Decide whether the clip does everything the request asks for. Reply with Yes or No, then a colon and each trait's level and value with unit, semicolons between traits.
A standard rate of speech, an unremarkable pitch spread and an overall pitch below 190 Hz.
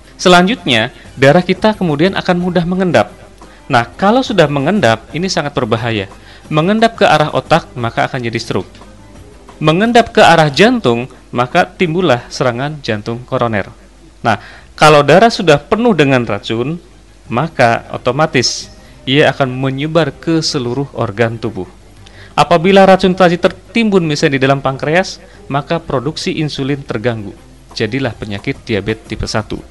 No: average, 130 wpm; wide, 7.2 semitones; medium, 140 Hz